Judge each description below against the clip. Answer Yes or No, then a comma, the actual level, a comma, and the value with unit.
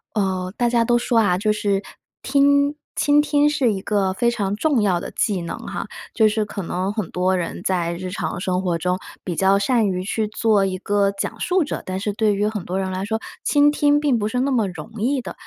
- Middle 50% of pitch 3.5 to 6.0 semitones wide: Yes, average, 4.2 semitones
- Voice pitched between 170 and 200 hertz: No, high, 210 Hz